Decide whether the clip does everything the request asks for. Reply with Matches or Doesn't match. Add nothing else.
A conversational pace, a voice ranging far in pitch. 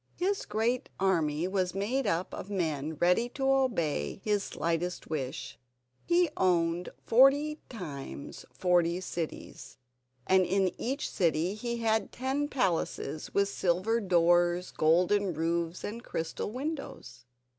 Doesn't match